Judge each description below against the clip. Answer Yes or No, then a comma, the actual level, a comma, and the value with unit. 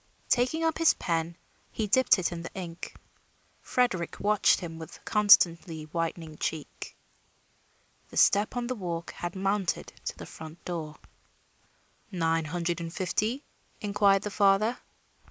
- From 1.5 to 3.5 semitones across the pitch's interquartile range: No, average, 3.9 semitones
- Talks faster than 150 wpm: No, slow, 135 wpm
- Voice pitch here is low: No, medium, 180 Hz